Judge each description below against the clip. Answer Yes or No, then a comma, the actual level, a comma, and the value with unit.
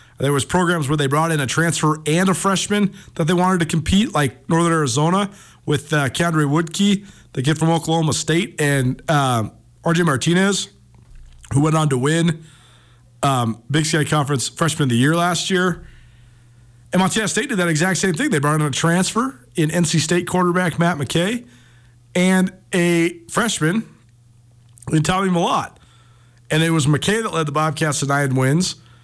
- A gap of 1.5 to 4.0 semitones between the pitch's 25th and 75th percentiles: No, average, 4.6 semitones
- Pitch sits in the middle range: Yes, medium, 160 Hz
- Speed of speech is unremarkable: Yes, average, 175 wpm